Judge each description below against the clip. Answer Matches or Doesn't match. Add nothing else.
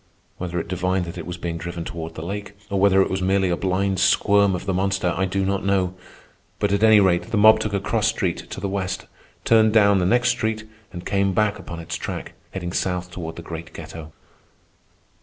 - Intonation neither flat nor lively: Doesn't match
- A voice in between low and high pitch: Doesn't match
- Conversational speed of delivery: Doesn't match